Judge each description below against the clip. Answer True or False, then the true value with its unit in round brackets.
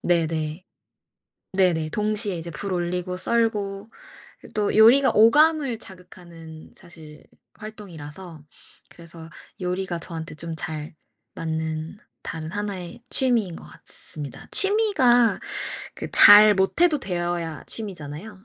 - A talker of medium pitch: True (180 Hz)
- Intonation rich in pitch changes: False (4.7 semitones)